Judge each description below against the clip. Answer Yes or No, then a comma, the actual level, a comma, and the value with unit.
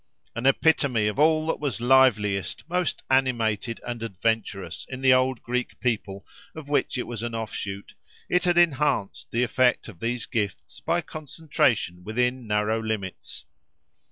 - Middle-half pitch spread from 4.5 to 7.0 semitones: No, average, 4.0 semitones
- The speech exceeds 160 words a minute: No, average, 150 wpm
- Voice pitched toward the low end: Yes, low, 120 Hz